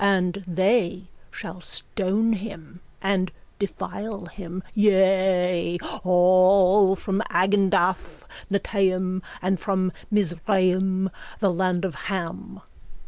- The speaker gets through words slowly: Yes, slow, 90 wpm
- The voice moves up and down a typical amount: No, narrow, 1.5 semitones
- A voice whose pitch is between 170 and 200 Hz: Yes, high, 190 Hz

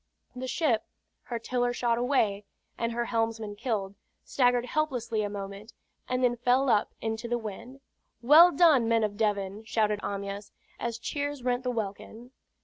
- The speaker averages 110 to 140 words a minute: No, average, 155 wpm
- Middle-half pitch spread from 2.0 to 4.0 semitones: Yes, average, 2.8 semitones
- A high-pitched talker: Yes, high, 235 Hz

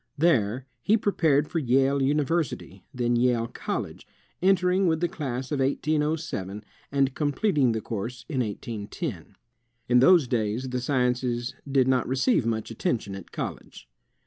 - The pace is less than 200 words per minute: Yes, average, 145 wpm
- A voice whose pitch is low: Yes, low, 130 Hz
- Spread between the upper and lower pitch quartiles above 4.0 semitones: Yes, average, 4.4 semitones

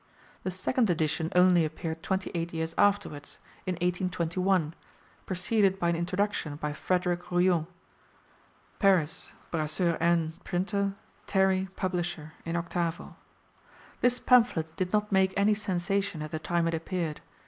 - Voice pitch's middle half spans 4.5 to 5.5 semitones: No, average, 2.7 semitones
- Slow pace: Yes, slow, 130 wpm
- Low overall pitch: No, medium, 175 Hz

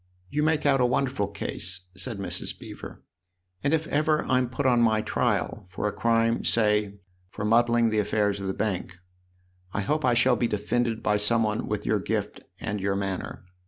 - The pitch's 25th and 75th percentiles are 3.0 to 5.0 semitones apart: Yes, average, 3.5 semitones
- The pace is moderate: Yes, average, 195 wpm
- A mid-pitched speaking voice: No, low, 110 Hz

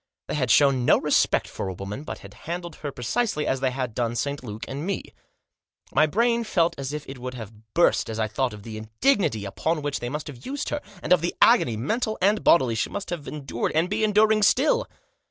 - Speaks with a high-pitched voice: No, medium, 145 Hz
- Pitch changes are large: Yes, wide, 7.8 semitones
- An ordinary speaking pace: No, fast, 225 wpm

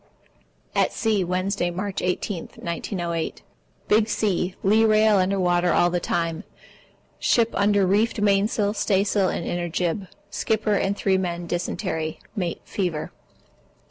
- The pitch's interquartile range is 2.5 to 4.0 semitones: Yes, average, 2.9 semitones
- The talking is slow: Yes, slow, 130 wpm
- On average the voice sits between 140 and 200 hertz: Yes, high, 190 Hz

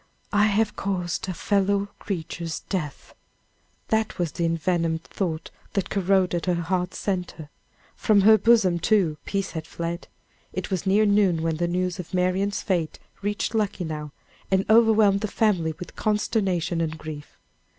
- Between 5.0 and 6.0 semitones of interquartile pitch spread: No, average, 3.3 semitones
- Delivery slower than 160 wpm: Yes, average, 150 wpm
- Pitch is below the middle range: No, medium, 185 Hz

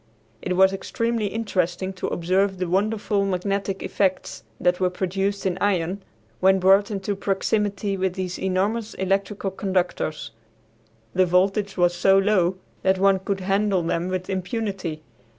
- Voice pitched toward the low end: No, high, 190 Hz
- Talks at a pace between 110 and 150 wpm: Yes, average, 140 wpm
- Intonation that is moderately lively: No, narrow, 1.5 semitones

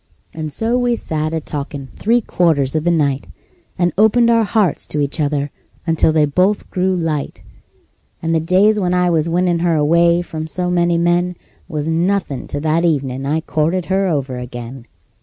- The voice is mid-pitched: Yes, medium, 165 Hz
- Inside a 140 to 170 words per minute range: No, average, 180 wpm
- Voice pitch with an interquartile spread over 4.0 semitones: No, average, 3.4 semitones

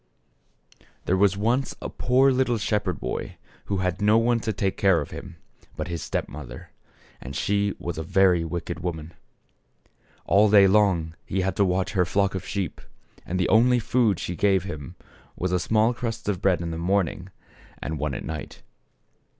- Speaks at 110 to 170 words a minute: No, average, 185 wpm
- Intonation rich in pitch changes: No, average, 3.5 semitones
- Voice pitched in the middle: No, very low, 95 Hz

